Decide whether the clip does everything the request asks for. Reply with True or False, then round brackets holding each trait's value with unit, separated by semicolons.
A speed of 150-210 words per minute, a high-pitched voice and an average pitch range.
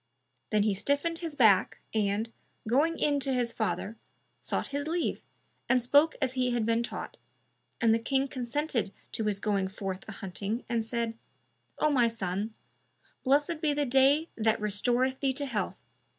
True (165 wpm; 240 Hz; 4.6 semitones)